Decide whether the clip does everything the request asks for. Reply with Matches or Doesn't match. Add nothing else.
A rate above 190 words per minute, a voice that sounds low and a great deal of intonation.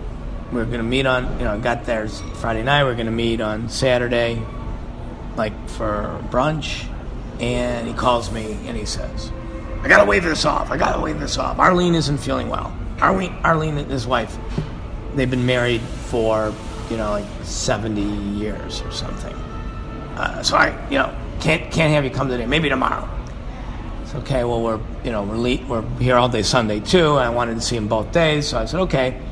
Doesn't match